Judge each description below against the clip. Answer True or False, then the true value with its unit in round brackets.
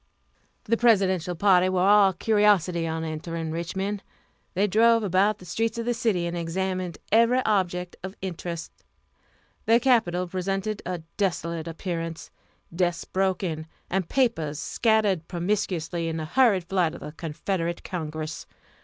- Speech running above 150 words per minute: False (135 wpm)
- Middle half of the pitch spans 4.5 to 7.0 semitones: False (3.5 semitones)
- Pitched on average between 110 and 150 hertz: False (185 Hz)